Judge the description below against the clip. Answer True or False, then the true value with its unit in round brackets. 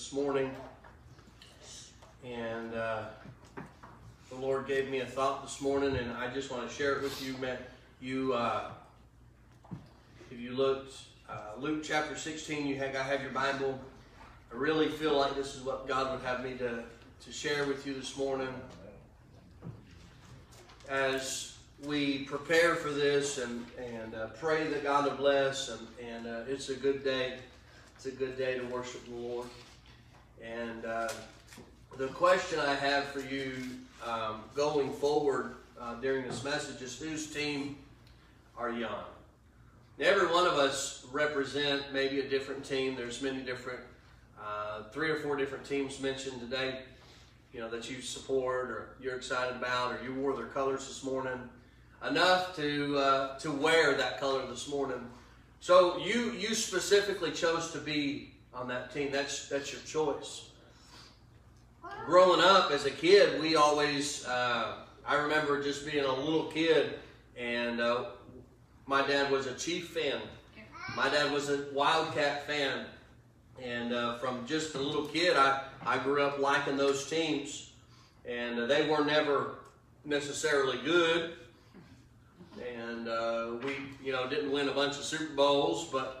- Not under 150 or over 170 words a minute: True (155 wpm)